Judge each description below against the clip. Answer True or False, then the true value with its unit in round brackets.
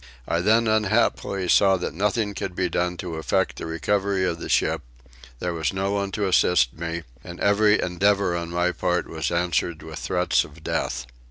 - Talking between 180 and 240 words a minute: True (185 wpm)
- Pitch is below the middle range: True (90 Hz)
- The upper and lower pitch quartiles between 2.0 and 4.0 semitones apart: True (2.8 semitones)